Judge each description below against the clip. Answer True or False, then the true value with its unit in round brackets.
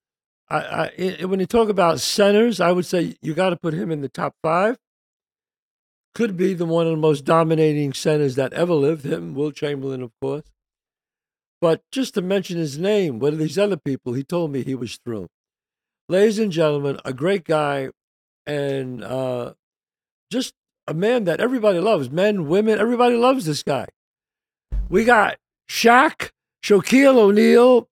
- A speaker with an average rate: True (170 wpm)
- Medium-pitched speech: True (175 Hz)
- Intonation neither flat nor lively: False (6.3 semitones)